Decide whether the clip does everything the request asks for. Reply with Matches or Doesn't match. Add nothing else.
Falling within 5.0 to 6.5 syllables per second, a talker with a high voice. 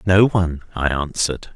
Doesn't match